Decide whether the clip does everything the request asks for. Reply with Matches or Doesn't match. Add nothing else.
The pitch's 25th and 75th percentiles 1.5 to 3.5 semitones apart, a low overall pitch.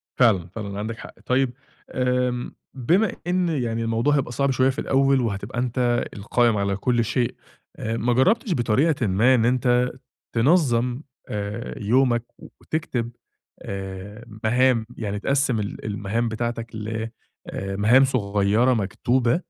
Matches